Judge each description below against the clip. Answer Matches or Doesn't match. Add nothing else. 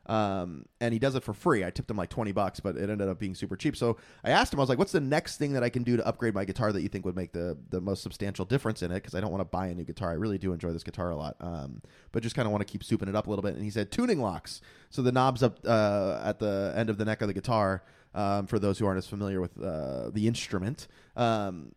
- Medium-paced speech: Doesn't match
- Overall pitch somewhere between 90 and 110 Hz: Matches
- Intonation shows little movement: Doesn't match